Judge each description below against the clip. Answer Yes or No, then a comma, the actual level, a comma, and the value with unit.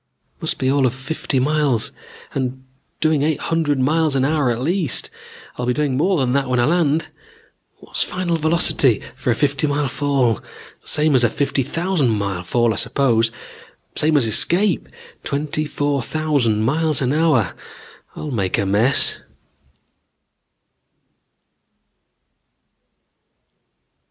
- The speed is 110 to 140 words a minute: Yes, slow, 135 wpm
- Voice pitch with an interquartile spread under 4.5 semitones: Yes, average, 3.8 semitones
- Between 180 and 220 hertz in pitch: No, medium, 140 Hz